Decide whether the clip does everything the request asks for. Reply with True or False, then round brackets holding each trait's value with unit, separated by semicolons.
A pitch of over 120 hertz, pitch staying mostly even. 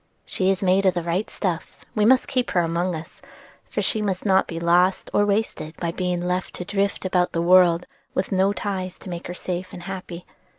True (185 Hz; 1.8 semitones)